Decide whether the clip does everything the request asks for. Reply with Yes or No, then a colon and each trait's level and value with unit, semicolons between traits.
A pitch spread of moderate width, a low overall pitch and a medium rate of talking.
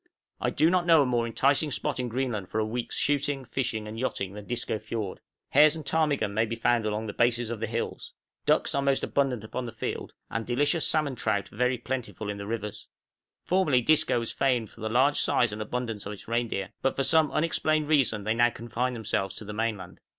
No: average, 4.1 semitones; low, 120 Hz; fast, 215 wpm